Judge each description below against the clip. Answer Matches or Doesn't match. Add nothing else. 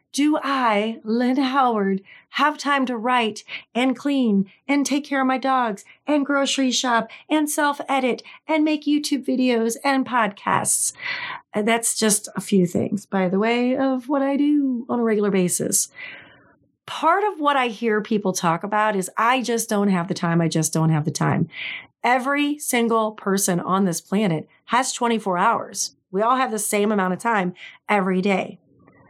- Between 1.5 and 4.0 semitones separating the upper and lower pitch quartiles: Doesn't match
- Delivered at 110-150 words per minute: Doesn't match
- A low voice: Doesn't match